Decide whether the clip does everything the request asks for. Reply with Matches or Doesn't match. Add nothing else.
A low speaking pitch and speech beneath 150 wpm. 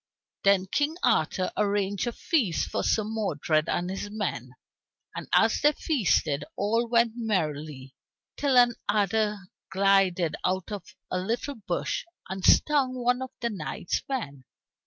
Doesn't match